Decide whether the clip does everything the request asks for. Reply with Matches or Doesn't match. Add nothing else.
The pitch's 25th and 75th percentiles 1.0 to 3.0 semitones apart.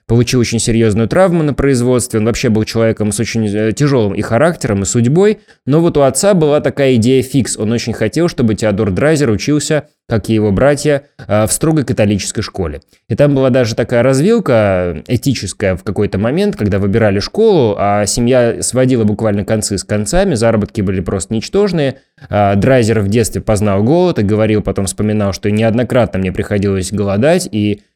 Doesn't match